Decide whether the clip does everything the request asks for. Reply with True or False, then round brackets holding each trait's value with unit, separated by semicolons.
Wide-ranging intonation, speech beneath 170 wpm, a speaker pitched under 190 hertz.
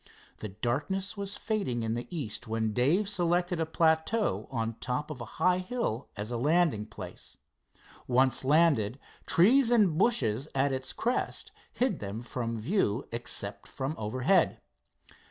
True (7.6 semitones; 150 wpm; 140 Hz)